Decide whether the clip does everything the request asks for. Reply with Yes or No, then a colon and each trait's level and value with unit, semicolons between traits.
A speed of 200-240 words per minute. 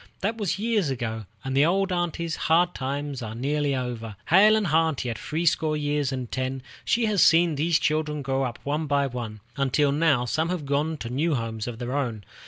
Yes: fast, 205 wpm